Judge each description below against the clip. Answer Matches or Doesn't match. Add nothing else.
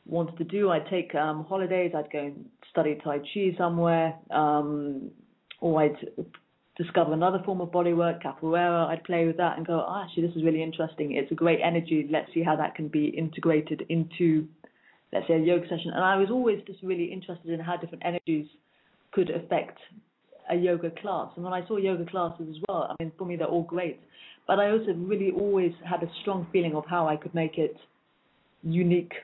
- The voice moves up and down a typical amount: Doesn't match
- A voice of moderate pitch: Matches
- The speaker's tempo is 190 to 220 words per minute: Matches